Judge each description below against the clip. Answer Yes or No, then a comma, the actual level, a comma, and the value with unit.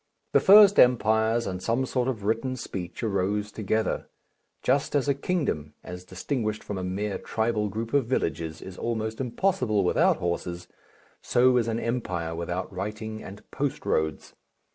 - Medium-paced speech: Yes, average, 155 wpm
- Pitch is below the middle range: Yes, low, 110 Hz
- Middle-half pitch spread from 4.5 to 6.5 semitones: Yes, average, 4.9 semitones